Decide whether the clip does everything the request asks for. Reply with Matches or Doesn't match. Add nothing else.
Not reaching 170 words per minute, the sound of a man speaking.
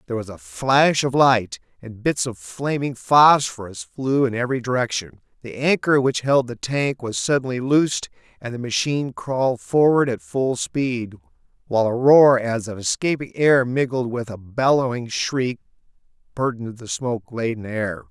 Matches